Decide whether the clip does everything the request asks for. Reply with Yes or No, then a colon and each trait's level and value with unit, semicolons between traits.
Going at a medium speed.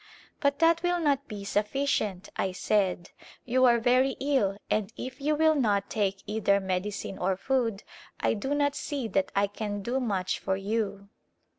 Yes: average, 180 wpm